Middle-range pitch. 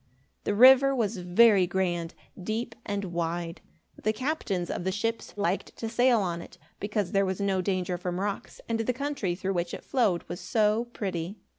No: high, 200 Hz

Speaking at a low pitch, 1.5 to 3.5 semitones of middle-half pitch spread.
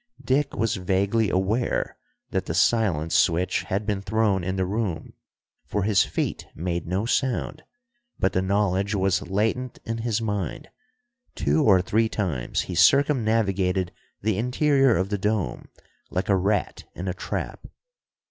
Yes: low, 100 Hz; average, 3.2 semitones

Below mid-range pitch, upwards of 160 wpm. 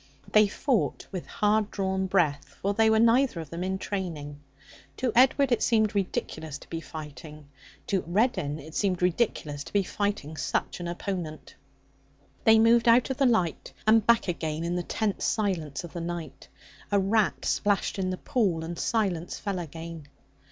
No: high, 190 Hz; average, 175 wpm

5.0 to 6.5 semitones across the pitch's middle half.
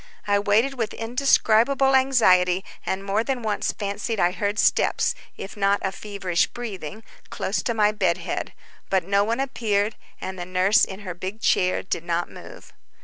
No: average, 3.2 semitones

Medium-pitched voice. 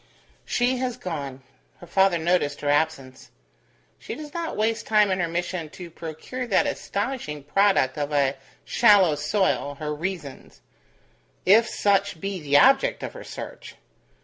Yes: medium, 175 Hz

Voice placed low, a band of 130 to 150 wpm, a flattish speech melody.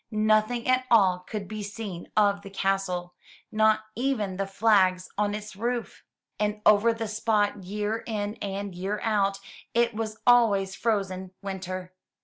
No: high, 205 Hz; average, 145 wpm; narrow, 2.1 semitones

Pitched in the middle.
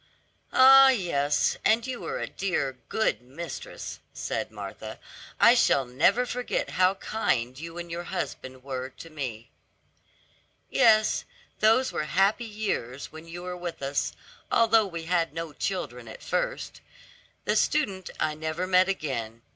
Yes: medium, 175 Hz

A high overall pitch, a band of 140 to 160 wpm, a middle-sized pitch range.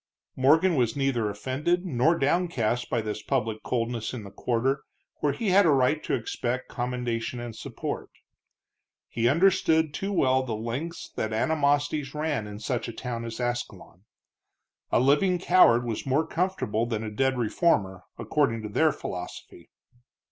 No: low, 125 Hz; average, 155 wpm; average, 5.0 semitones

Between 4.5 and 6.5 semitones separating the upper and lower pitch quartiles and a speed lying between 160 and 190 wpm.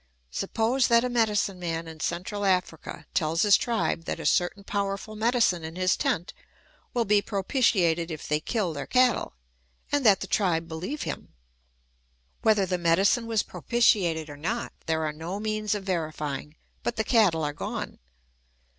Yes: average, 5.1 semitones; average, 165 wpm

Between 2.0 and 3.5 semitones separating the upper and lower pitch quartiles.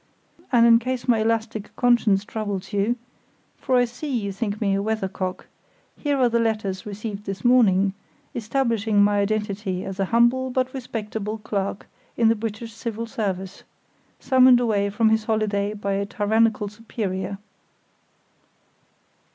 Yes: narrow, 2.6 semitones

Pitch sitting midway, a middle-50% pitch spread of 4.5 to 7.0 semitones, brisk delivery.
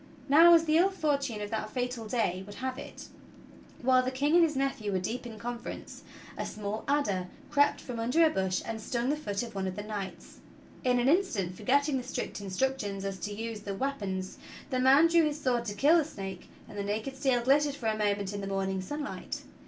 No: high, 240 Hz; wide, 5.5 semitones; fast, 225 wpm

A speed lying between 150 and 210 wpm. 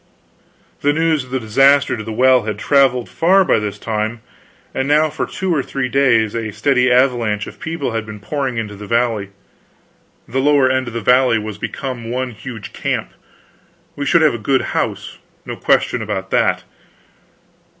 Yes: average, 180 wpm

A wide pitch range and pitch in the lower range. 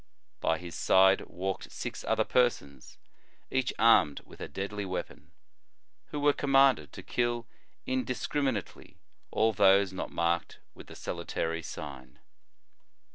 Yes: wide, 6.7 semitones; low, 100 Hz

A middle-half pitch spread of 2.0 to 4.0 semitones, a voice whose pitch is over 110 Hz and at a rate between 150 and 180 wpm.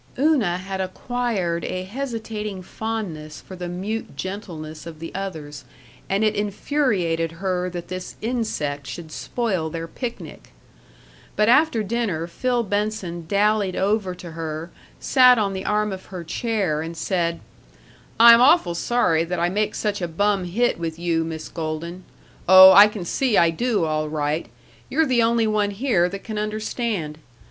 No: average, 4.5 semitones; high, 190 Hz; average, 155 wpm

